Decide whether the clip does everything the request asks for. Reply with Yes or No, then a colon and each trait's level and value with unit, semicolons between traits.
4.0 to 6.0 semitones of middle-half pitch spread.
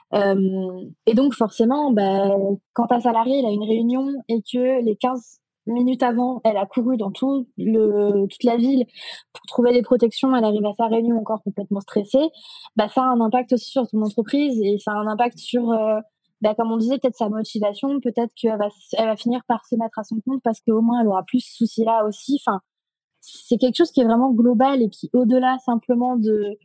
No: average, 2.9 semitones